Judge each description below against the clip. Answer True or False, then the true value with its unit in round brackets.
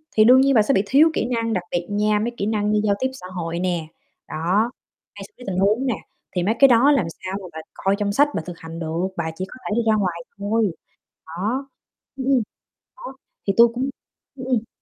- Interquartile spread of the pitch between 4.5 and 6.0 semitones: True (5.2 semitones)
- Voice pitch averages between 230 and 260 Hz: False (210 Hz)